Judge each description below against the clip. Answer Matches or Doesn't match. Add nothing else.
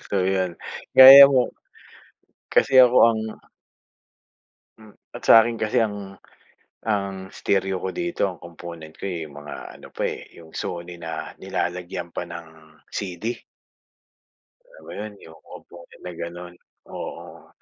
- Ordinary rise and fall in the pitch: Matches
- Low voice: Matches